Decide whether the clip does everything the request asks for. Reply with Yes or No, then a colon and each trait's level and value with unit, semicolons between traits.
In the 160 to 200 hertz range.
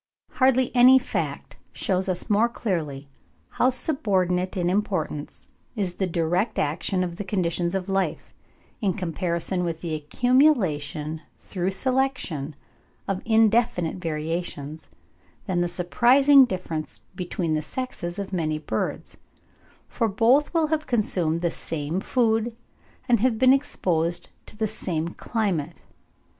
Yes: medium, 185 Hz